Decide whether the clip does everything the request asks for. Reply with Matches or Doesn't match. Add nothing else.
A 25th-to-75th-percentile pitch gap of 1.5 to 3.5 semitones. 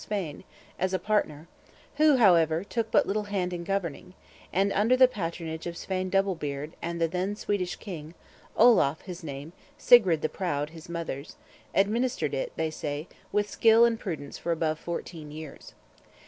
Doesn't match